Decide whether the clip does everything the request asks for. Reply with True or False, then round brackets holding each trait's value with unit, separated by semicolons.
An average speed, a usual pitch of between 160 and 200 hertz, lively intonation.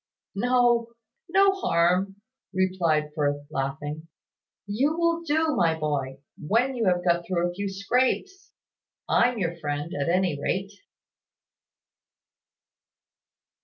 False (110 wpm; 185 Hz; 7.9 semitones)